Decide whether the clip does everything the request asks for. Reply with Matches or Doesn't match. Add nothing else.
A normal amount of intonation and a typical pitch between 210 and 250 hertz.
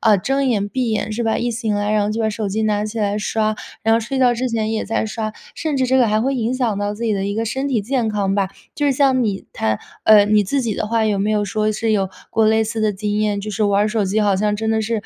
Doesn't match